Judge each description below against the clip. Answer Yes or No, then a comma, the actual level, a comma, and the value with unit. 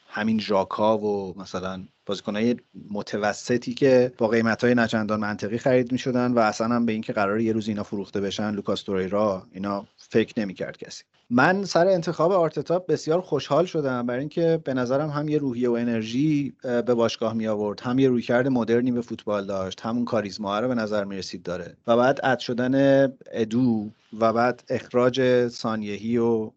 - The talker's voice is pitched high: No, low, 120 Hz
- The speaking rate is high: Yes, fast, 165 wpm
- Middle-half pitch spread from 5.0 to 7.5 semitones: No, average, 3.2 semitones